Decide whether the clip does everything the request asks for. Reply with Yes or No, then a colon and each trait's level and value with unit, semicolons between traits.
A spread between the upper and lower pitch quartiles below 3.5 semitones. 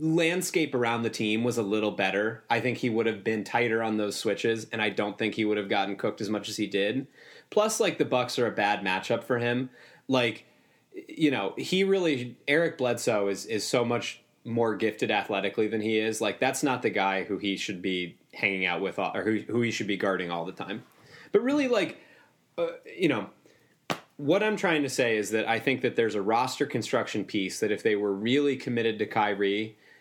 No: average, 4.2 semitones